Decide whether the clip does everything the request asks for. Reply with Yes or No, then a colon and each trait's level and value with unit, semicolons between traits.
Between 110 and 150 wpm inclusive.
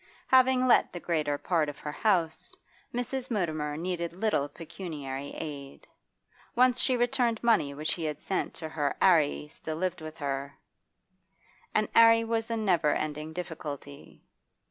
Yes: average, 145 wpm